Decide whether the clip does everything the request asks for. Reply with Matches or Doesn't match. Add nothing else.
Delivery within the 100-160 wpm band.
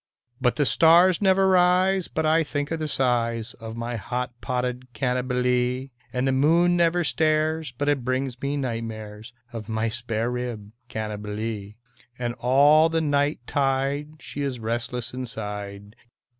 Matches